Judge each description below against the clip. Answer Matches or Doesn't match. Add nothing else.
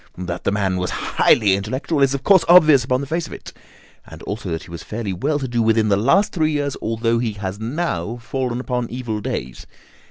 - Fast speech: Matches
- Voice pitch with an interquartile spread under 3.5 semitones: Doesn't match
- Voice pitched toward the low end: Matches